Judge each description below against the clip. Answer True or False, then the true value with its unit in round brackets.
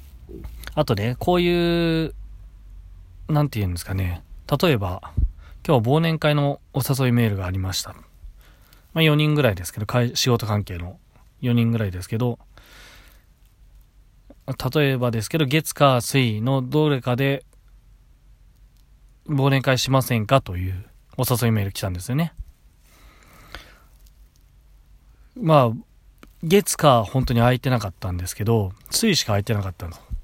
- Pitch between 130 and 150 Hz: False (120 Hz)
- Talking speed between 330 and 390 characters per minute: False (265 characters per minute)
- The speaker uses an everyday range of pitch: False (7.0 semitones)